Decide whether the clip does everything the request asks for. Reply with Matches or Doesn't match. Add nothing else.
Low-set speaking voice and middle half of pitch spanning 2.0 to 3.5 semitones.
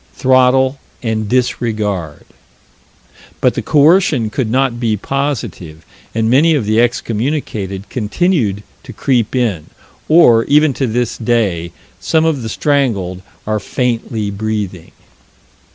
Doesn't match